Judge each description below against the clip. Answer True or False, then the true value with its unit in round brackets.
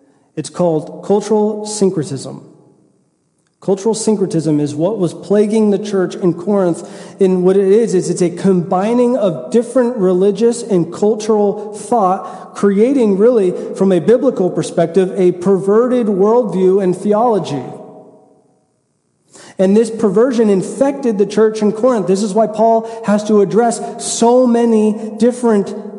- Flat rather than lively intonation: False (3.4 semitones)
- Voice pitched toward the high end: True (205 Hz)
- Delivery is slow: True (130 wpm)